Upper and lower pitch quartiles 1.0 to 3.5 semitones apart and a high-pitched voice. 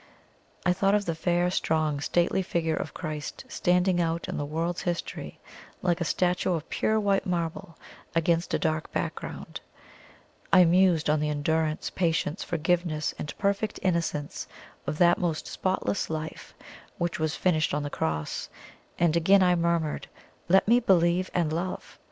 No: narrow, 2.4 semitones; medium, 170 Hz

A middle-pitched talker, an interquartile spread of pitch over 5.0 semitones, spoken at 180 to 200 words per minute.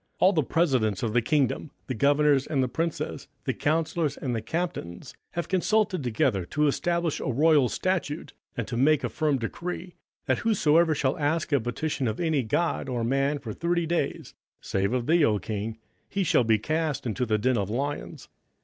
Yes: medium, 145 Hz; wide, 5.5 semitones; average, 190 wpm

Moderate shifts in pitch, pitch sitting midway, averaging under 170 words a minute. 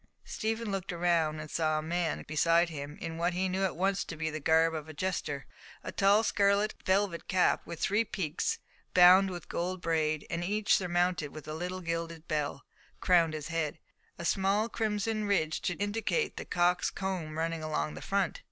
No: average, 3.5 semitones; medium, 175 Hz; average, 190 wpm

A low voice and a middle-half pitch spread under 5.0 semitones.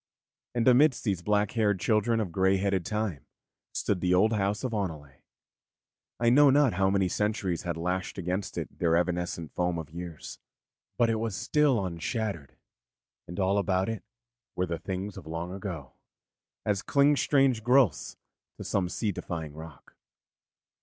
Yes: very low, 95 Hz; average, 4.1 semitones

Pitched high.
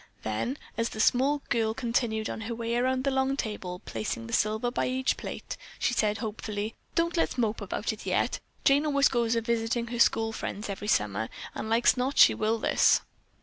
Yes: high, 230 Hz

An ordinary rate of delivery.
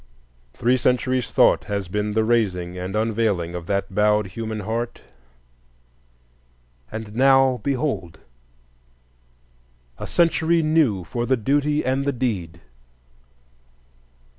No: slow, 110 wpm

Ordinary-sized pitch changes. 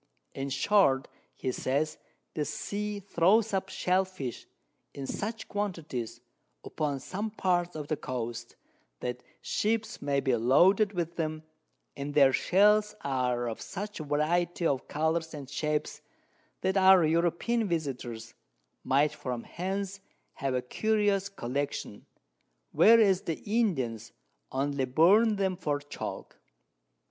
No: wide, 6.3 semitones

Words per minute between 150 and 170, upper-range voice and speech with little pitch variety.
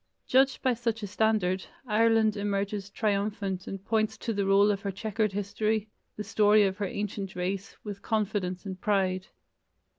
Yes: average, 160 wpm; high, 205 Hz; narrow, 1.8 semitones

